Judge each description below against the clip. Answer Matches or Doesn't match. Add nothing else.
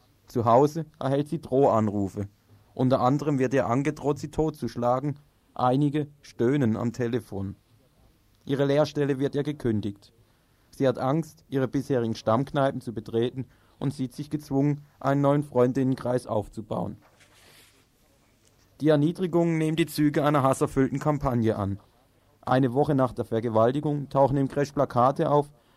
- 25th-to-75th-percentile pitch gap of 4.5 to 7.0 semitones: Doesn't match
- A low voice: Matches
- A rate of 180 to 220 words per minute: Doesn't match